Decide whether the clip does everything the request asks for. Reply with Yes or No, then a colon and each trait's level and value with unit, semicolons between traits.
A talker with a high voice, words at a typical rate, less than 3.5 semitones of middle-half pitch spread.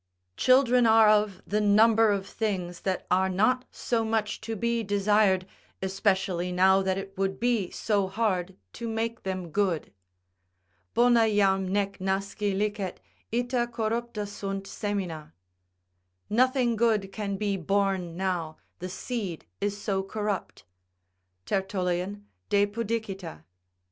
No: high, 200 Hz; slow, 125 wpm; narrow, 2.6 semitones